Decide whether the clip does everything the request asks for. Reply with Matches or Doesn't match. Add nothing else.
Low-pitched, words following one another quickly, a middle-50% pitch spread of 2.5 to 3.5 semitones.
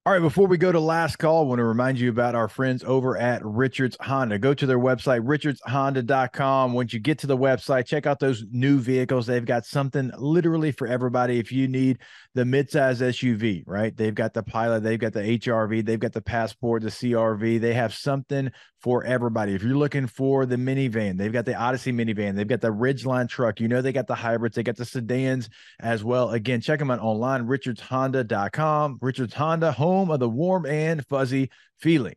Matches